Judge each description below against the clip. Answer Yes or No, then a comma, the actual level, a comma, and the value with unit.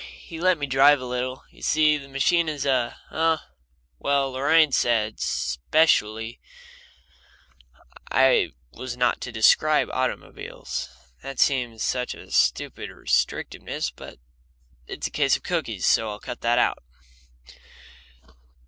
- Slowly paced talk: Yes, slow, 130 wpm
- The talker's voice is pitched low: Yes, low, 130 Hz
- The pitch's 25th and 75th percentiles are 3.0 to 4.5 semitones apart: Yes, average, 3.6 semitones